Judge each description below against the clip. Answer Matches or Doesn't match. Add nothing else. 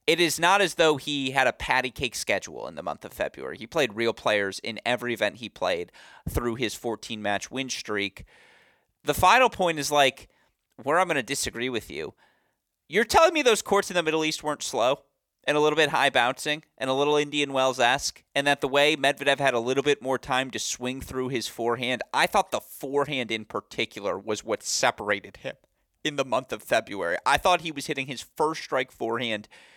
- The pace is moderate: Doesn't match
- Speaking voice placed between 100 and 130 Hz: Doesn't match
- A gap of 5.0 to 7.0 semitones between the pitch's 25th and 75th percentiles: Doesn't match